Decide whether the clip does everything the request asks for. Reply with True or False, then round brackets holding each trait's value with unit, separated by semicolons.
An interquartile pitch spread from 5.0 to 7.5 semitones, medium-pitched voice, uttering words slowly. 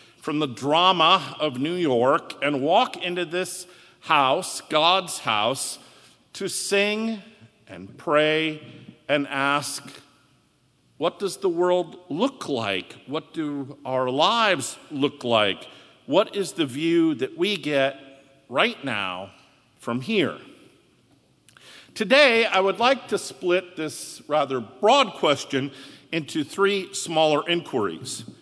True (5.5 semitones; 155 Hz; 120 wpm)